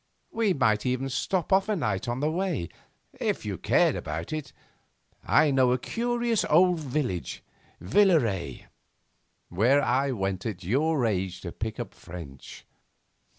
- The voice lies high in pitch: No, low, 130 Hz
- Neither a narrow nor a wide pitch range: No, wide, 8.8 semitones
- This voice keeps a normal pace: Yes, average, 145 wpm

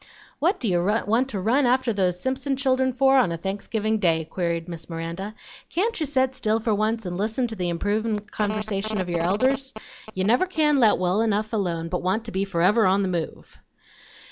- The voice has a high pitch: Yes, high, 215 Hz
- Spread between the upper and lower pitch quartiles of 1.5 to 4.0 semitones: No, wide, 5.6 semitones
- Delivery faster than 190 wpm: Yes, average, 200 wpm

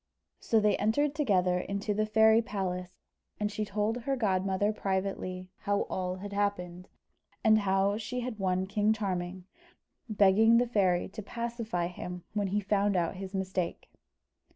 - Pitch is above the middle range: Yes, high, 200 Hz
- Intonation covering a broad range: No, narrow, 2.6 semitones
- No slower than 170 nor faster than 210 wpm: No, average, 155 wpm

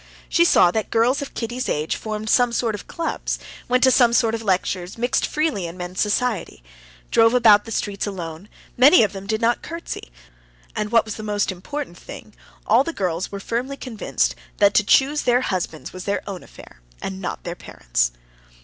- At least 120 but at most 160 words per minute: No, average, 195 wpm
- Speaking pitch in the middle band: No, high, 215 Hz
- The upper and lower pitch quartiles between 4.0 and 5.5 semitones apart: Yes, average, 4.6 semitones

